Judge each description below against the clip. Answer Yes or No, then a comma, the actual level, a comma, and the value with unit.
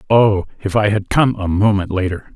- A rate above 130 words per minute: Yes, fast, 205 wpm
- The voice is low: Yes, low, 100 Hz